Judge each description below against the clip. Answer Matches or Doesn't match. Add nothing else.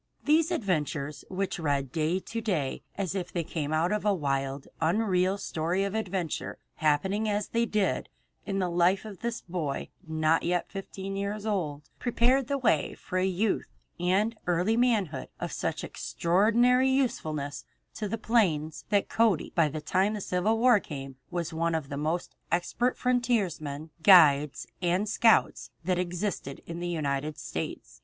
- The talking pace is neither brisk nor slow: Matches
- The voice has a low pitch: Doesn't match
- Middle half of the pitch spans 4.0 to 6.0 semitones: Matches